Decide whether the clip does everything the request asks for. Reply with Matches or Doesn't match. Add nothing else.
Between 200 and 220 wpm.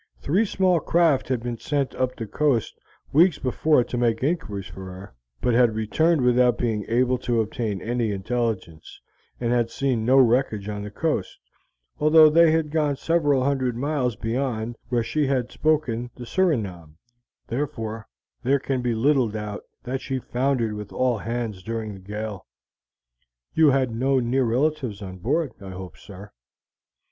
Doesn't match